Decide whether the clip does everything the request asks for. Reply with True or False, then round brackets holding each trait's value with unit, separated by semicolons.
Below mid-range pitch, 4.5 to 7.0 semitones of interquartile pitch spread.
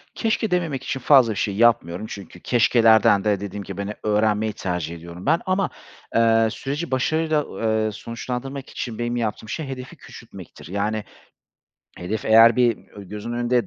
False (115 Hz; 3.9 semitones)